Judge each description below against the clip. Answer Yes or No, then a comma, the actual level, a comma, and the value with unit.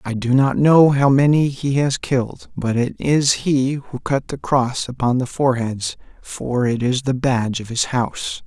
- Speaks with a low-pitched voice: Yes, low, 130 Hz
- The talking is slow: No, average, 200 wpm